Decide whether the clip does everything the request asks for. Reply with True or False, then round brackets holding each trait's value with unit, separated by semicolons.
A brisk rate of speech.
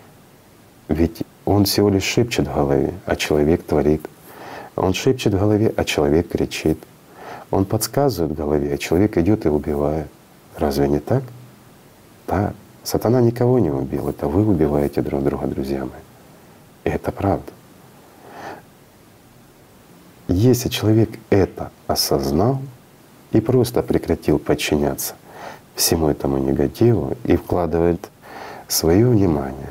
False (120 wpm)